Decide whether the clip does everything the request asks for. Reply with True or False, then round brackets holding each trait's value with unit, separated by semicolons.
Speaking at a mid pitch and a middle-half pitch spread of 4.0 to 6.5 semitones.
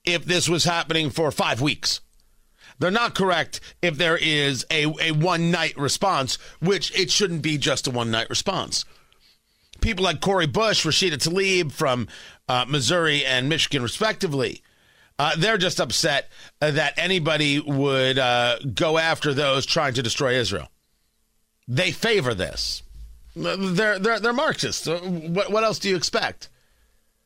True (160 Hz; 5.3 semitones)